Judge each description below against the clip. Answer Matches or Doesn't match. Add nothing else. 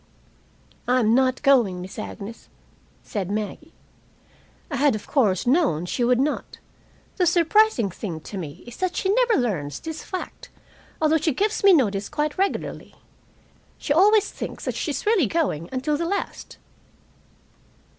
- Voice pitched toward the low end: Doesn't match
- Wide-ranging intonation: Matches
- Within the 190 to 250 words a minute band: Doesn't match